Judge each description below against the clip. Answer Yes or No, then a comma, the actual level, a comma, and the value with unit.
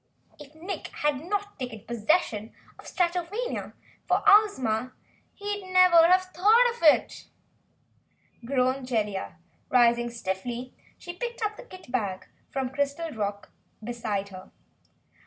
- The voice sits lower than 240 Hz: No, very high, 275 Hz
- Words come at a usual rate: No, slow, 125 wpm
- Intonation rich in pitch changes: Yes, wide, 7.9 semitones